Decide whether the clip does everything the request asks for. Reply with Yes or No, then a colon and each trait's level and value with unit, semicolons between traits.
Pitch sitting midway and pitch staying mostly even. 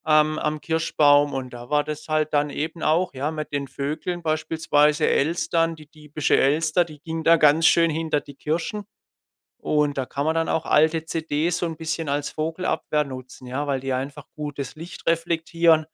Yes: medium, 155 Hz; narrow, 2.0 semitones